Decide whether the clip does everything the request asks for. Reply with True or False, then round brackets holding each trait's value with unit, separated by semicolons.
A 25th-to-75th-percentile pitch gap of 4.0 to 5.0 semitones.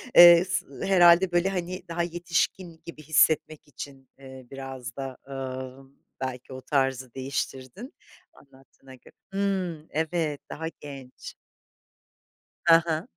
True (4.6 semitones)